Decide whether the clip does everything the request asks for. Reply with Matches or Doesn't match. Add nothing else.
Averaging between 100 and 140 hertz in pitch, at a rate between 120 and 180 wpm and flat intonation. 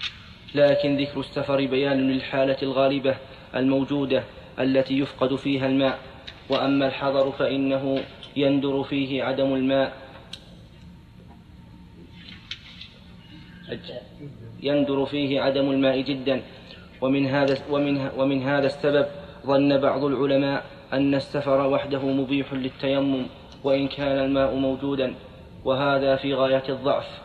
Doesn't match